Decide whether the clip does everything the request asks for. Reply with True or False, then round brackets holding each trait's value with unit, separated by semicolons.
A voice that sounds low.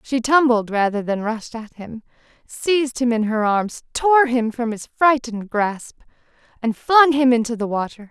False (240 Hz)